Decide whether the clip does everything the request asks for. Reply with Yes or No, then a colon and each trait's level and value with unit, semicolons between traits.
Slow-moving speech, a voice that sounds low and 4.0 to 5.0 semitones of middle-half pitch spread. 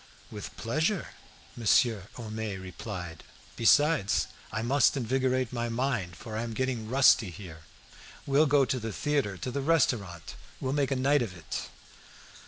No: average, 150 wpm; low, 120 Hz; average, 4.7 semitones